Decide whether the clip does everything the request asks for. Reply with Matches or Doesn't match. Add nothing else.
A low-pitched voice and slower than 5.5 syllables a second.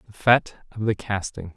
Doesn't match